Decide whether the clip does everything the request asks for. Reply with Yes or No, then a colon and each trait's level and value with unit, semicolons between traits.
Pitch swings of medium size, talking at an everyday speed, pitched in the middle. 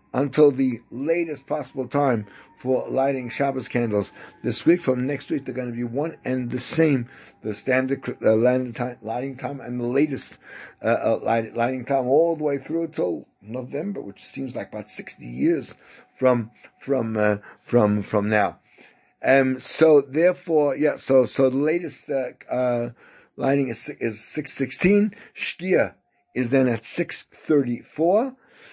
No: average, 3.5 semitones; average, 155 wpm; low, 130 Hz